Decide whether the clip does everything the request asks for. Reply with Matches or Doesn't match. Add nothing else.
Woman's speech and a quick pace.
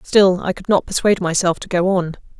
Matches